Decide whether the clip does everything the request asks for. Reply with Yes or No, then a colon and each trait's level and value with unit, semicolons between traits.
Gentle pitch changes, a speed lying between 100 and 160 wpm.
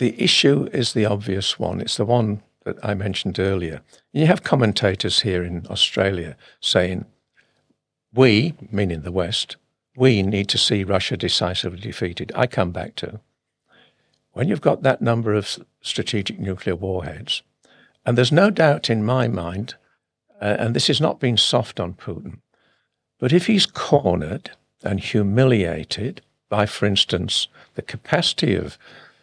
No: average, 4.4 semitones; average, 150 wpm